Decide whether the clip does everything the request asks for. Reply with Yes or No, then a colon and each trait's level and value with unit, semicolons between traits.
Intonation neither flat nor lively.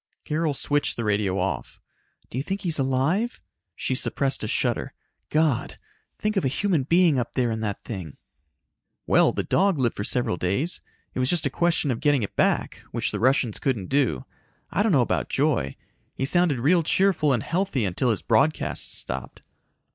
No: wide, 6.6 semitones